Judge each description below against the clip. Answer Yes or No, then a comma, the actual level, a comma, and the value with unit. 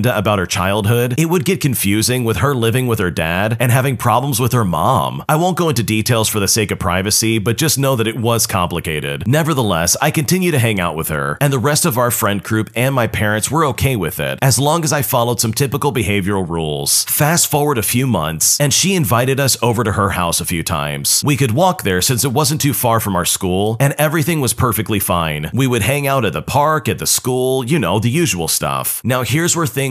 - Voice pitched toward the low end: Yes, low, 120 Hz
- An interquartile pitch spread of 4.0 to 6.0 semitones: Yes, wide, 5.6 semitones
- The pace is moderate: No, fast, 240 wpm